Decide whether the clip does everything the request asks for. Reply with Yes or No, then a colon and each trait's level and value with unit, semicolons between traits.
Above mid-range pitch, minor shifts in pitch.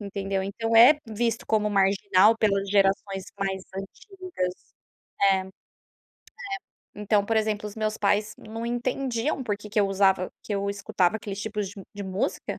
Yes: high, 205 Hz; narrow, 2.1 semitones